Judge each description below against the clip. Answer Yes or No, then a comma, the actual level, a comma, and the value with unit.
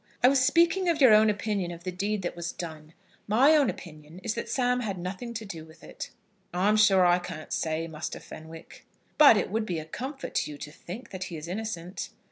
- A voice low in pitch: No, high, 190 Hz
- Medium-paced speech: No, fast, 225 wpm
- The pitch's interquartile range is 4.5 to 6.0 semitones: Yes, average, 5.2 semitones